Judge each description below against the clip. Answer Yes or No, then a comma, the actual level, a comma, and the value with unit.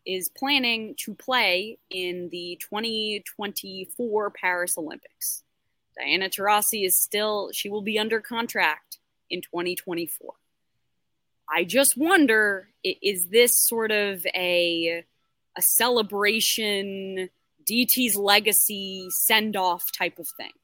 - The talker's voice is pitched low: No, high, 205 Hz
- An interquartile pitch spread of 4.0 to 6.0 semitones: No, average, 3.6 semitones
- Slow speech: Yes, slow, 105 wpm